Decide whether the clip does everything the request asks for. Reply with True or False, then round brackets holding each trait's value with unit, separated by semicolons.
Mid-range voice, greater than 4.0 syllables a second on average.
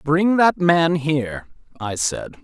False (155 Hz; 3.6 syllables/s)